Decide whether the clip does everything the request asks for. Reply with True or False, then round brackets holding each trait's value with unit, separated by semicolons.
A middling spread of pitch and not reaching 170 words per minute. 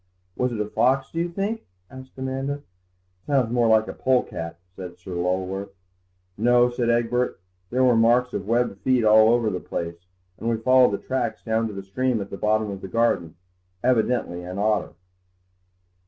False (4.2 semitones; 180 wpm)